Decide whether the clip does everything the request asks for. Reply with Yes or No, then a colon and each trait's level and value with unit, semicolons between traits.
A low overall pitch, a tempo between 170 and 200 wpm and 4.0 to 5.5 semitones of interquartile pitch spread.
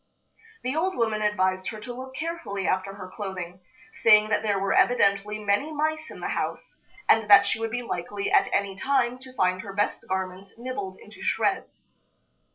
No: high, 210 Hz; average, 180 wpm; average, 4.5 semitones